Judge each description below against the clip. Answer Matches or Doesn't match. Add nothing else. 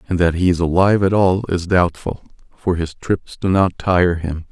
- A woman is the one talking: Doesn't match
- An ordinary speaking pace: Doesn't match